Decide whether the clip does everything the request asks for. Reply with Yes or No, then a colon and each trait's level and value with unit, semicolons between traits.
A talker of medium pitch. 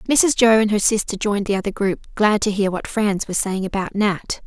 No: high, 205 Hz